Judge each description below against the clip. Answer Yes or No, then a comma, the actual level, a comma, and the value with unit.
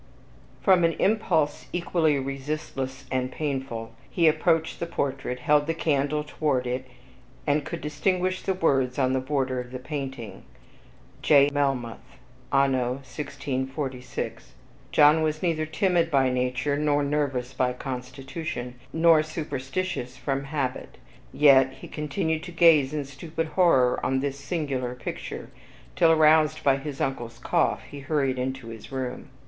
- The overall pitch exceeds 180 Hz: No, medium, 140 Hz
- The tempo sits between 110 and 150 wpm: Yes, average, 140 wpm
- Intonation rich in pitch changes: No, average, 3.2 semitones